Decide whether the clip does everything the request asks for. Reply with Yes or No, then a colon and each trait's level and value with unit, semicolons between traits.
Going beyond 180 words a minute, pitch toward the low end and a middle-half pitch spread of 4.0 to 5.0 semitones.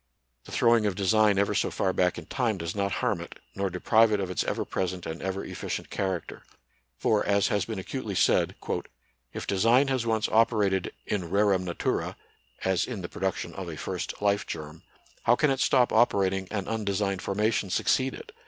No: average, 190 wpm; low, 100 Hz; average, 2.9 semitones